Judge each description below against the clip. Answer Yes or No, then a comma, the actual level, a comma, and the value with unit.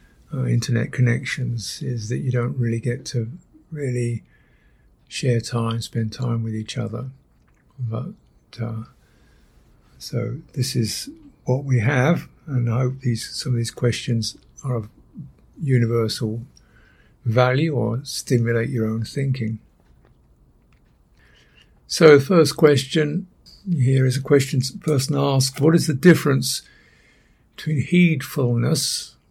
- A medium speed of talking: No, slow, 125 wpm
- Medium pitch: No, low, 125 Hz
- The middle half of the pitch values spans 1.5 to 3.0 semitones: No, average, 3.4 semitones